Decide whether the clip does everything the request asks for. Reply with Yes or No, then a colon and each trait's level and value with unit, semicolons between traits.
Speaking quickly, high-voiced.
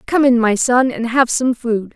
Yes: fast, 245 wpm; high, 245 Hz